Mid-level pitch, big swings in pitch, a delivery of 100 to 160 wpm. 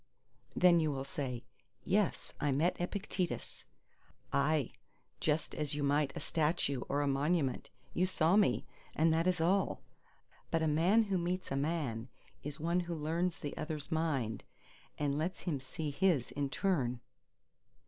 No: medium, 155 Hz; average, 3.8 semitones; average, 155 wpm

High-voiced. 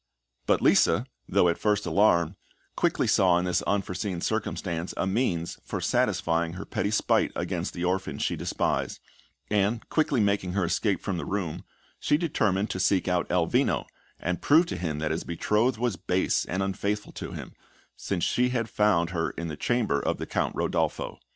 No: very low, 95 Hz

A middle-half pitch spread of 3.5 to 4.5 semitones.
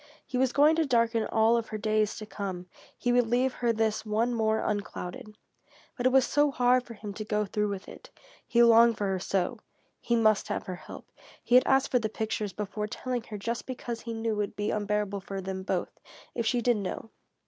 No: narrow, 2.6 semitones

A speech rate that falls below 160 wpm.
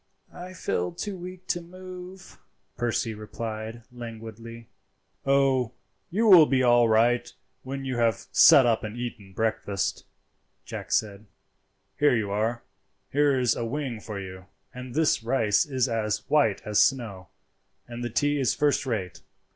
Yes: average, 145 wpm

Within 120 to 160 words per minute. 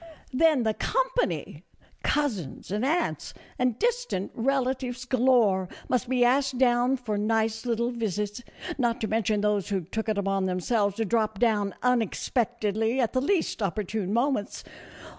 Yes: average, 140 wpm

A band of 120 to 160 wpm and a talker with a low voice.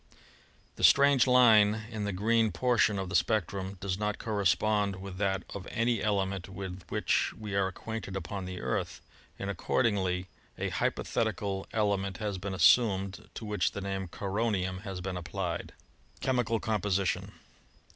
Yes: average, 155 wpm; low, 100 Hz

